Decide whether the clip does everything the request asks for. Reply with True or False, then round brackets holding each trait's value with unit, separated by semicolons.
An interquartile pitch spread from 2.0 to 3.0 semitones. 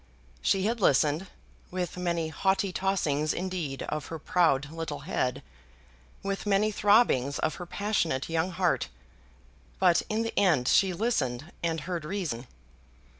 False (4.5 semitones)